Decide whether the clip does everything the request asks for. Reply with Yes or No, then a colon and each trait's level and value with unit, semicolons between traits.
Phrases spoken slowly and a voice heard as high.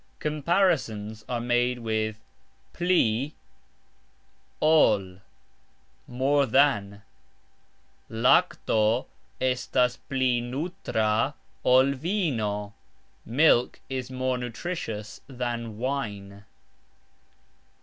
No: slow, 65 wpm; low, 125 Hz